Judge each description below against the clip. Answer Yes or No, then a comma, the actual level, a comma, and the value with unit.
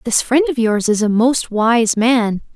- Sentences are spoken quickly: Yes, fast, 210 wpm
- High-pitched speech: Yes, high, 230 Hz